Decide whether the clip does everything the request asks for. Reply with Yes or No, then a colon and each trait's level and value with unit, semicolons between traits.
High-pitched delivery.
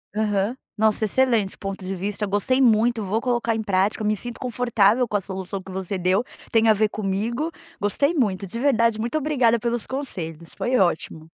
Yes: high, 215 Hz